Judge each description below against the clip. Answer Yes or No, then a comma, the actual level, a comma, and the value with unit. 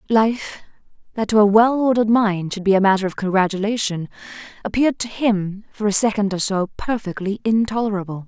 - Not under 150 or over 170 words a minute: Yes, average, 165 wpm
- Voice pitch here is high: Yes, high, 210 Hz